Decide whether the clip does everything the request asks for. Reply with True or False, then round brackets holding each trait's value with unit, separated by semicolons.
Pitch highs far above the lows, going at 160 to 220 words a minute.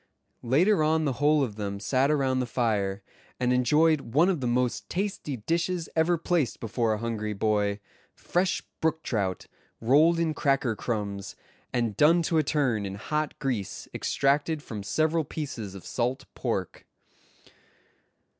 False (6.2 semitones; 145 wpm)